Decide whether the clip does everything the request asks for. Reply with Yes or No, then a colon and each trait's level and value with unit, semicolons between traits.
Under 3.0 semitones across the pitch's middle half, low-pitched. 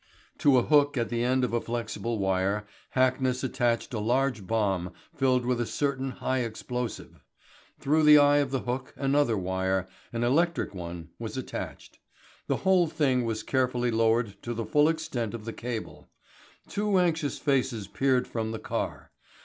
No: average, 3.4 semitones; low, 125 Hz